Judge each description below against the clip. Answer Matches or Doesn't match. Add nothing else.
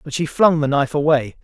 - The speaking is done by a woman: Doesn't match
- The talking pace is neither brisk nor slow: Doesn't match